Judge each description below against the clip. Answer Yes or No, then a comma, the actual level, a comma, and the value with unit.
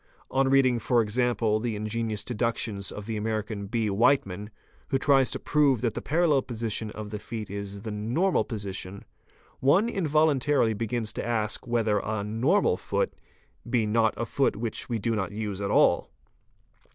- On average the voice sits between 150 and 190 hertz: No, low, 115 Hz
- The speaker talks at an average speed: Yes, average, 170 wpm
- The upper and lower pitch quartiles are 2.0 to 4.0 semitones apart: Yes, average, 3.2 semitones